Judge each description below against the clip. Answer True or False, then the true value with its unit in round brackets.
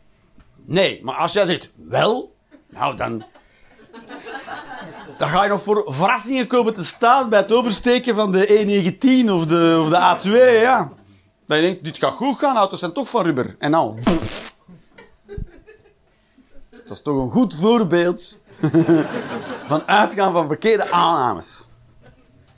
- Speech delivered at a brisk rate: False (145 wpm)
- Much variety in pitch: True (6.4 semitones)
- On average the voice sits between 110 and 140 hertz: False (190 Hz)